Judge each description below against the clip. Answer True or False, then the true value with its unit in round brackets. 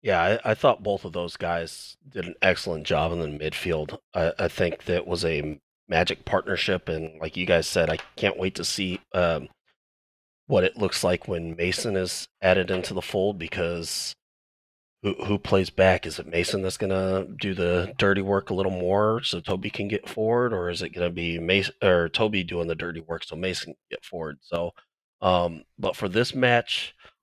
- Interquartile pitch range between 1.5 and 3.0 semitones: True (2.4 semitones)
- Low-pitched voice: True (90 Hz)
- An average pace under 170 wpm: False (200 wpm)